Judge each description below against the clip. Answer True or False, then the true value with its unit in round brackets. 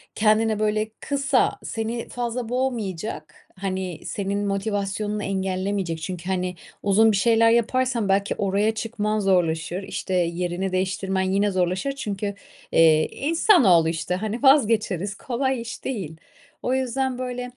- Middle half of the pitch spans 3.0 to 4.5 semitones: True (3.8 semitones)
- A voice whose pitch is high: True (205 Hz)